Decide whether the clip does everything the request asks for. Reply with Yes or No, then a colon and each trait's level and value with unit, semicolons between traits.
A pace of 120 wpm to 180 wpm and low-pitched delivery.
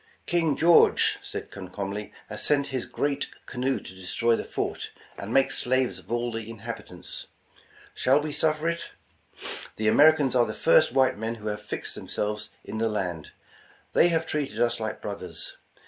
Yes: average, 170 wpm; low, 120 Hz